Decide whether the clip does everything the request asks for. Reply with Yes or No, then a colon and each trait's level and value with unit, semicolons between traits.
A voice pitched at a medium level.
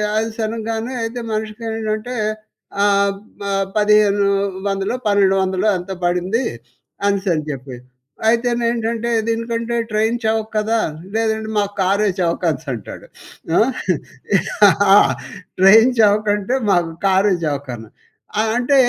No: high, 215 Hz